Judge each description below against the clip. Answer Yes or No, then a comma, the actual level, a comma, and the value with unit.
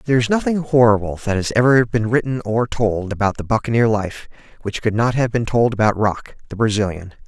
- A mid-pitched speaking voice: No, low, 115 Hz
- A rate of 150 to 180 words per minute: No, fast, 205 wpm